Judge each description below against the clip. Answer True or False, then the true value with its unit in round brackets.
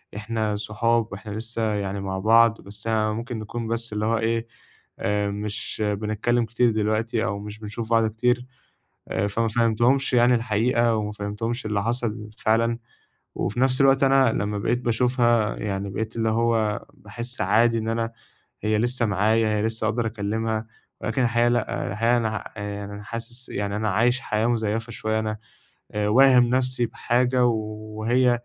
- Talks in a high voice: False (110 Hz)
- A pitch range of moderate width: False (2.0 semitones)